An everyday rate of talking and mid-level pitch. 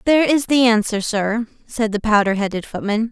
No: average, 190 wpm; high, 225 Hz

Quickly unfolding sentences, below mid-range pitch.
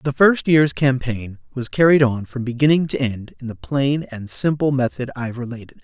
No: average, 195 wpm; low, 130 Hz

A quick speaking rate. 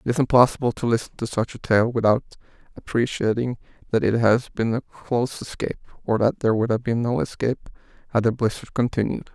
No: average, 195 wpm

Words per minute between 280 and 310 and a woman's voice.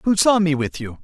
No: fast, 290 wpm; male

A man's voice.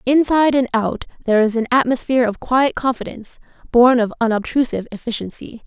No: female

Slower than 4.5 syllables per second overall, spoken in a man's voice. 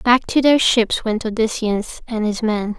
No: 4.1 syllables/s; female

